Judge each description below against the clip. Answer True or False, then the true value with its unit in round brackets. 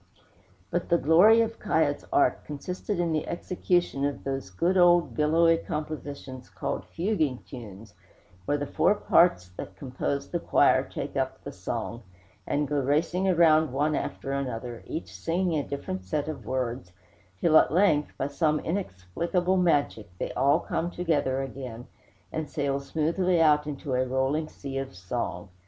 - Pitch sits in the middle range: True (150 Hz)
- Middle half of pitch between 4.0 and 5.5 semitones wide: True (4.5 semitones)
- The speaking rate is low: False (155 wpm)